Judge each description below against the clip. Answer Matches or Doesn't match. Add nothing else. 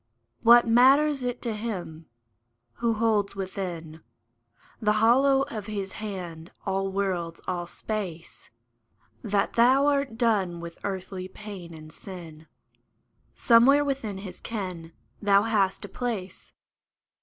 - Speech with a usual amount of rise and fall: Matches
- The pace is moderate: Doesn't match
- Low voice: Doesn't match